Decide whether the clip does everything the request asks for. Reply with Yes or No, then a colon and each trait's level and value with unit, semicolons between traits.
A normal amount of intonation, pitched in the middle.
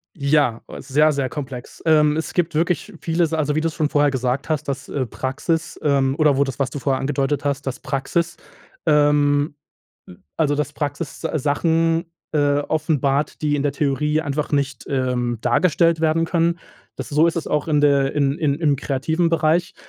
No: narrow, 2.3 semitones; medium, 145 Hz